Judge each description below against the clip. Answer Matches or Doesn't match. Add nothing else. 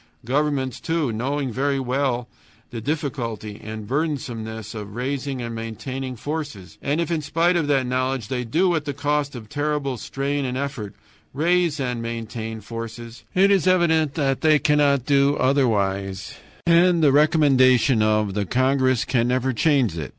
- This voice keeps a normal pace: Matches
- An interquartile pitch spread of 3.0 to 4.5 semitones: Matches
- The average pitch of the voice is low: Matches